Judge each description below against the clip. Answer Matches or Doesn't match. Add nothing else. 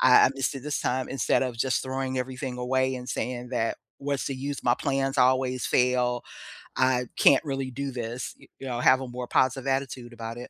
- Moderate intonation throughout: Doesn't match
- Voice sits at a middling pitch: Doesn't match